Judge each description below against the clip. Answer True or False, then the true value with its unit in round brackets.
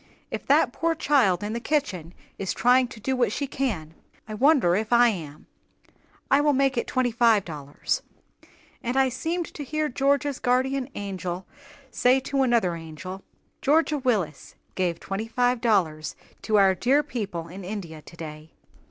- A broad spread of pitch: True (6.6 semitones)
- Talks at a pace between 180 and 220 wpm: False (160 wpm)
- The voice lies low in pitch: False (230 Hz)